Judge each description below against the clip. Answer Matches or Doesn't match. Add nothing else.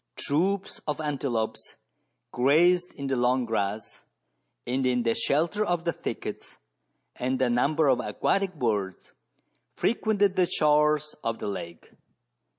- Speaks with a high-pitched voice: Doesn't match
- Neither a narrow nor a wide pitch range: Doesn't match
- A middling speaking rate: Doesn't match